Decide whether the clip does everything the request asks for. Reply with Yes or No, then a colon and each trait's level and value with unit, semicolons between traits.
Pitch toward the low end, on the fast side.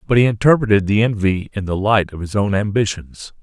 Yes: low, 105 Hz; fast, 210 wpm